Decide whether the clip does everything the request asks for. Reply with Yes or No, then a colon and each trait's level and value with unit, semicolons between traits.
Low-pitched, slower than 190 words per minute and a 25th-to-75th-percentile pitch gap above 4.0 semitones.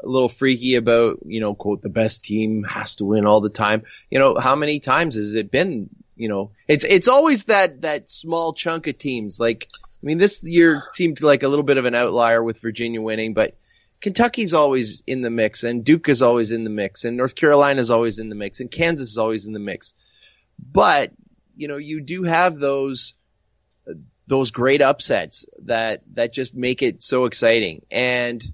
No: low, 125 Hz; average, 200 wpm; average, 5.1 semitones